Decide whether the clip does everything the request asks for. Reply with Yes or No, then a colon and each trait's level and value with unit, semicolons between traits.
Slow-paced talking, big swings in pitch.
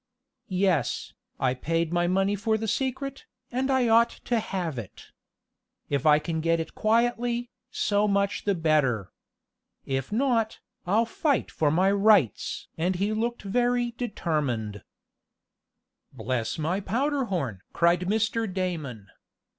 Yes: slow, 130 wpm; wide, 6.3 semitones